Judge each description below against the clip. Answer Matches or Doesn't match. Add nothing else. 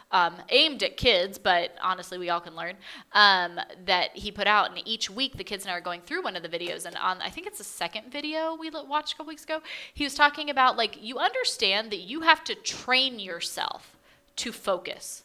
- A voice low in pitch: Doesn't match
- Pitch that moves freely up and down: Matches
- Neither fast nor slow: Doesn't match